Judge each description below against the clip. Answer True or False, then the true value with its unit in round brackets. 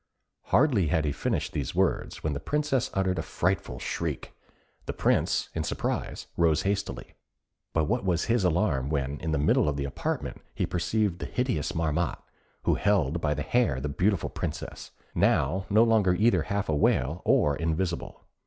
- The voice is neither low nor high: False (85 Hz)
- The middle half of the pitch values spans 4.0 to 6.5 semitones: True (5.3 semitones)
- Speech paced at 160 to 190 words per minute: True (170 wpm)